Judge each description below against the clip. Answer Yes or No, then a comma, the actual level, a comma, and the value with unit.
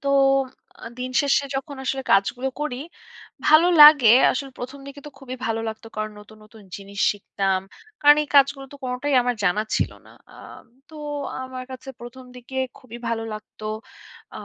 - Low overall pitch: No, very high, 255 Hz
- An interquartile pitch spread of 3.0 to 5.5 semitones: Yes, average, 4.2 semitones